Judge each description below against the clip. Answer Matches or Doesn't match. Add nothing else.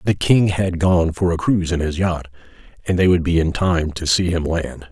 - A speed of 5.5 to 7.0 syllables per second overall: Doesn't match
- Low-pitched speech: Matches